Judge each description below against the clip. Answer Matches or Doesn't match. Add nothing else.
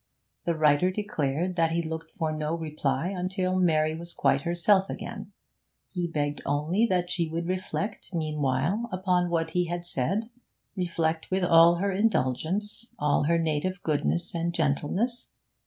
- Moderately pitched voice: Matches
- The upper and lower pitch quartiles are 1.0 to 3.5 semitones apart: Matches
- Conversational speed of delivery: Matches